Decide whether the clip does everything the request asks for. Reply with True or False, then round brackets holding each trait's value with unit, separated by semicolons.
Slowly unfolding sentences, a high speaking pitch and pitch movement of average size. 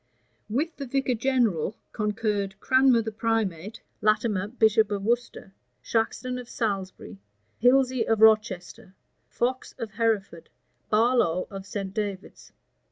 True (115 wpm; 220 Hz; 3.4 semitones)